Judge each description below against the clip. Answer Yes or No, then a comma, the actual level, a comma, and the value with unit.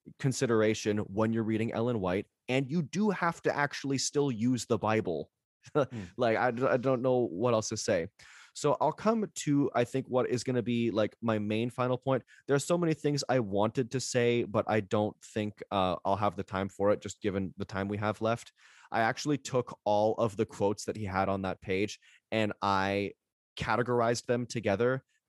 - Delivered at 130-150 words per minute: No, fast, 205 wpm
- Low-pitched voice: Yes, low, 115 Hz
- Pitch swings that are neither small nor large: Yes, average, 3.8 semitones